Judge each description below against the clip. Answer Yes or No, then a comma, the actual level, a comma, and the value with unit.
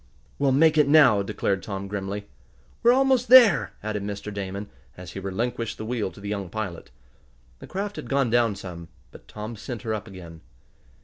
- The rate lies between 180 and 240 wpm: Yes, average, 185 wpm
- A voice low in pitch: Yes, low, 105 Hz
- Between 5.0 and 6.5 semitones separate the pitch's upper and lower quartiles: Yes, average, 5.3 semitones